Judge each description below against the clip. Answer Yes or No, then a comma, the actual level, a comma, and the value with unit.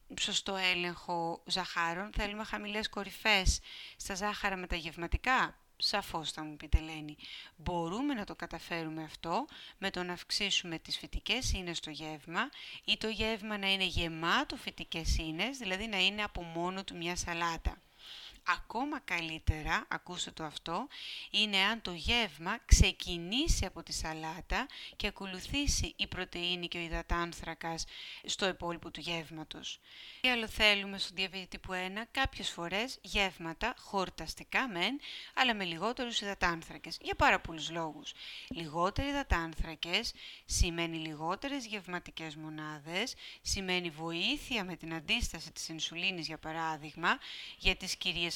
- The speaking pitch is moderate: Yes, medium, 180 Hz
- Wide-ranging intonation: No, average, 3.9 semitones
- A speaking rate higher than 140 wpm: No, average, 135 wpm